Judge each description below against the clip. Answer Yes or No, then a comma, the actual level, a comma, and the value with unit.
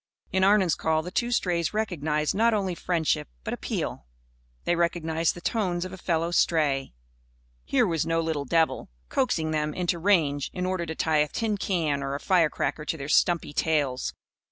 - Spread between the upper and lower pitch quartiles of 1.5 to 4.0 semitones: Yes, average, 3.3 semitones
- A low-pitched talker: No, medium, 165 Hz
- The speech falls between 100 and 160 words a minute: No, average, 180 wpm